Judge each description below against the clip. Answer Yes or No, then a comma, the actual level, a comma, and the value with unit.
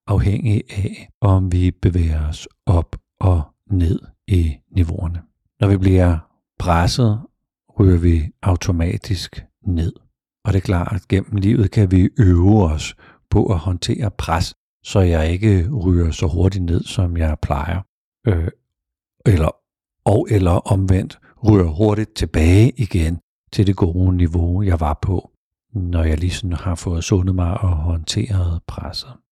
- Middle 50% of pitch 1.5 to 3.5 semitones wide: Yes, average, 3.0 semitones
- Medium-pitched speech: No, very low, 95 Hz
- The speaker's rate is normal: No, slow, 140 wpm